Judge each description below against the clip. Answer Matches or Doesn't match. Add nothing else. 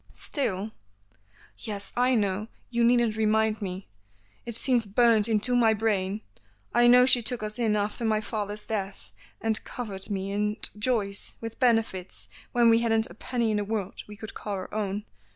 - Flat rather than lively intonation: Matches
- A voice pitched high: Matches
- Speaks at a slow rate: Doesn't match